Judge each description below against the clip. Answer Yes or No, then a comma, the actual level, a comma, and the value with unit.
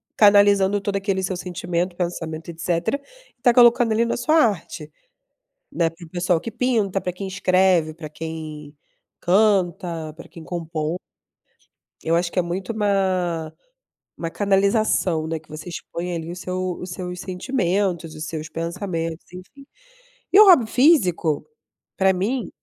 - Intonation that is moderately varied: Yes, average, 3.3 semitones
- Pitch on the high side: No, medium, 180 Hz